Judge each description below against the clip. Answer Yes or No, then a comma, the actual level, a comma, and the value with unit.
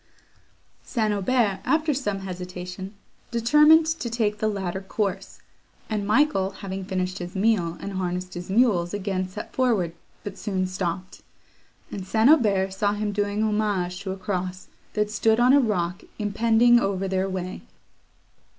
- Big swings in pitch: No, average, 2.9 semitones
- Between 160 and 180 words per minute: No, average, 150 wpm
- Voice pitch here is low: No, high, 200 Hz